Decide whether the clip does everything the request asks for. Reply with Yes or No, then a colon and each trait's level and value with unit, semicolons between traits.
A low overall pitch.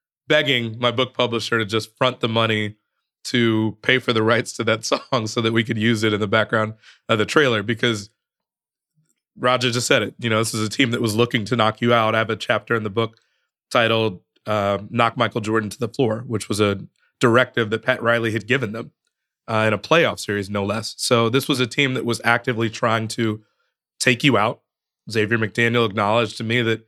Yes: low, 115 Hz